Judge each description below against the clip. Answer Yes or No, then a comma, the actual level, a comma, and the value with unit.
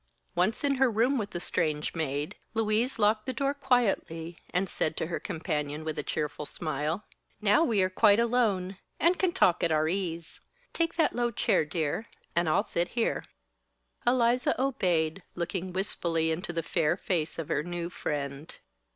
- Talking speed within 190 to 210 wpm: No, average, 170 wpm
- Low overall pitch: No, medium, 180 Hz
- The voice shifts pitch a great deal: Yes, wide, 6.3 semitones